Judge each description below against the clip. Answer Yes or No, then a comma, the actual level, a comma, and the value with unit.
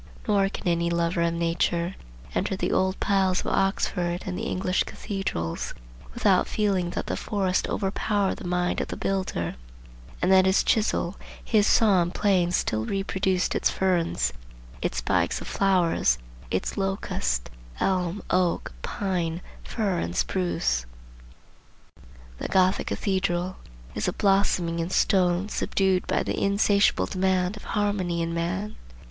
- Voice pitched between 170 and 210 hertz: Yes, medium, 185 Hz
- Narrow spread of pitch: Yes, narrow, 2.3 semitones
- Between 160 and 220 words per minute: No, average, 140 wpm